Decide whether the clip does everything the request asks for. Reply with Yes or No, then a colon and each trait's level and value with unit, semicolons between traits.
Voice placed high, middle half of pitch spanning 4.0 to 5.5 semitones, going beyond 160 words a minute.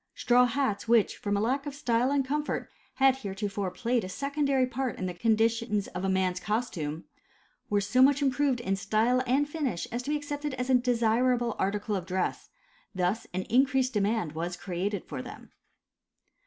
Yes: high, 235 Hz; average, 4.9 semitones; average, 175 wpm